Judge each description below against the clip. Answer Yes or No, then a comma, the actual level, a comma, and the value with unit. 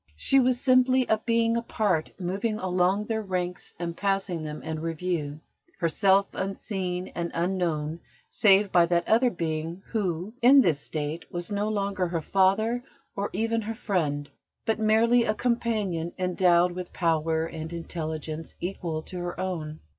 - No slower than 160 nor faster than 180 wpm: No, average, 150 wpm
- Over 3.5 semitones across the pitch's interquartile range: Yes, average, 4.5 semitones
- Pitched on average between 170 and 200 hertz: Yes, medium, 185 Hz